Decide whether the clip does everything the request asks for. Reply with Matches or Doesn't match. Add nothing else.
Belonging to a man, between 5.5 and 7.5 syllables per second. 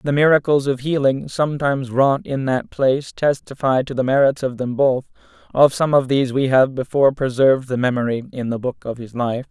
Matches